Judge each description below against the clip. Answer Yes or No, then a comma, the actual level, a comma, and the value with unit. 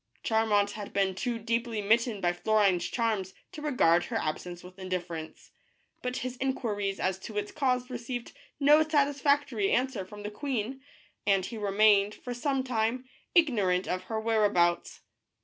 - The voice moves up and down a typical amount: Yes, average, 4.5 semitones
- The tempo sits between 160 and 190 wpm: No, average, 150 wpm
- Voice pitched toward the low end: No, high, 220 Hz